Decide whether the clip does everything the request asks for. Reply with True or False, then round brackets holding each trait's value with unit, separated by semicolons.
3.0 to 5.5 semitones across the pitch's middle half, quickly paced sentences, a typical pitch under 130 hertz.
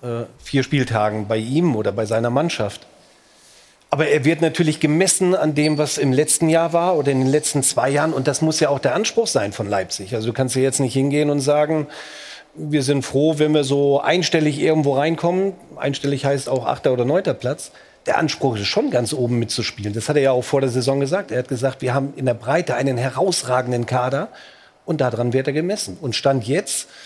False (3.4 semitones; 215 wpm; 140 Hz)